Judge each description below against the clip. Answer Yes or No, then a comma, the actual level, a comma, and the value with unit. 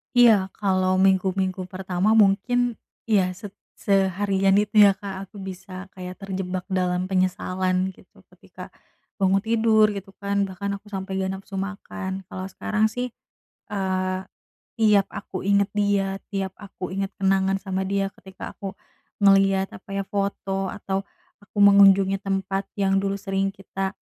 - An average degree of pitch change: No, narrow, 1.0 semitones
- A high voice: Yes, high, 195 Hz